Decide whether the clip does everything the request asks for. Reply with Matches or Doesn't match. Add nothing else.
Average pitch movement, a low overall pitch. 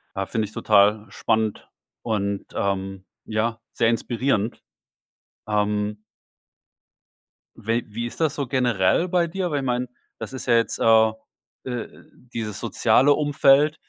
Matches